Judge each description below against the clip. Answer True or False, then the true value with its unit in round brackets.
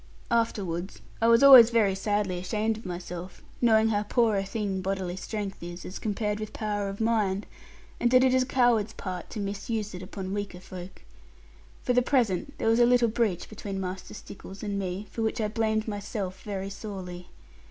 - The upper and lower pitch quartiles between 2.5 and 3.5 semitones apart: True (2.9 semitones)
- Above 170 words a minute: True (190 wpm)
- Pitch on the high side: True (205 Hz)